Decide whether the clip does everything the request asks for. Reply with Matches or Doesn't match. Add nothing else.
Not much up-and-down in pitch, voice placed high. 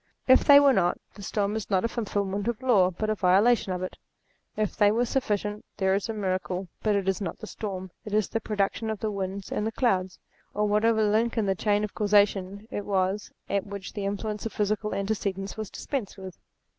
Matches